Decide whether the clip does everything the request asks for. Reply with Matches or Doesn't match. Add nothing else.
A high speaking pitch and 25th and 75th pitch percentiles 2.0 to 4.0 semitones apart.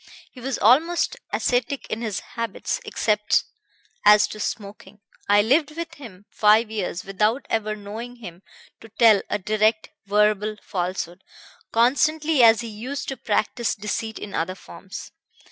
Matches